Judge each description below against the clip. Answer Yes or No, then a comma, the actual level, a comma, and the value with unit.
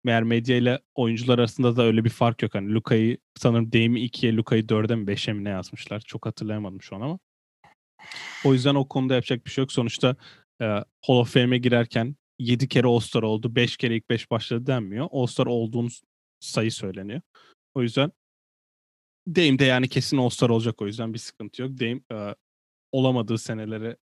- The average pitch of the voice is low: Yes, low, 120 Hz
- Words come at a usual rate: No, fast, 185 wpm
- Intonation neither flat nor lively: No, narrow, 2.2 semitones